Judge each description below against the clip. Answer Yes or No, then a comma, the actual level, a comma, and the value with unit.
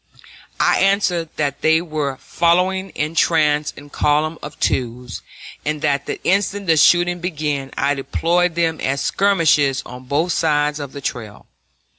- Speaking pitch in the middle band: Yes, medium, 155 Hz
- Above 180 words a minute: No, average, 150 wpm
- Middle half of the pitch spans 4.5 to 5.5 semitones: No, average, 3.5 semitones